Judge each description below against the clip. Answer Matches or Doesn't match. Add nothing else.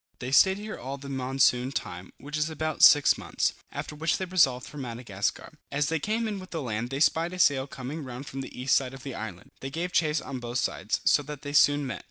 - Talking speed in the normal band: Doesn't match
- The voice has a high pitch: Doesn't match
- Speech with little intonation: Doesn't match